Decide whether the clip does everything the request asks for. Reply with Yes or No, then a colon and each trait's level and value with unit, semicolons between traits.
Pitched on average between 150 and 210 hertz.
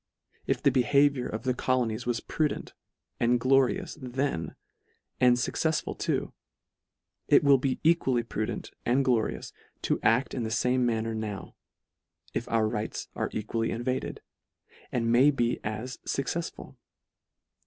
No: low, 125 Hz